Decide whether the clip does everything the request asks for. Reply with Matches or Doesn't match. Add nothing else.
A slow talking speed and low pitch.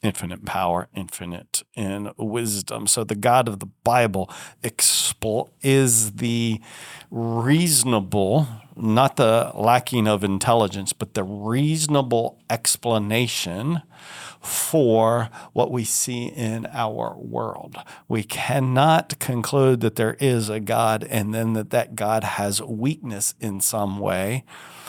Matches